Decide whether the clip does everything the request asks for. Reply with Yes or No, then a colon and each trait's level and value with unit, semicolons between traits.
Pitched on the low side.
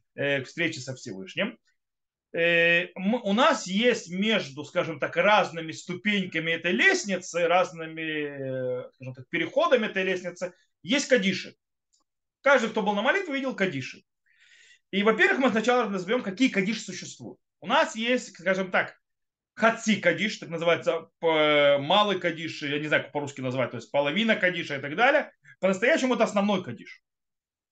No: medium, 185 Hz